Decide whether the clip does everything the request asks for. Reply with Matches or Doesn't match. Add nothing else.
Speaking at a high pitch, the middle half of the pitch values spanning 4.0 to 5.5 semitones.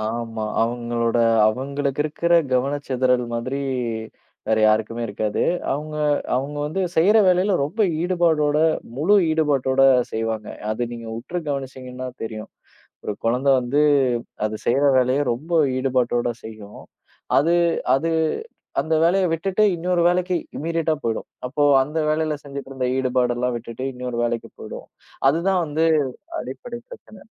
Doesn't match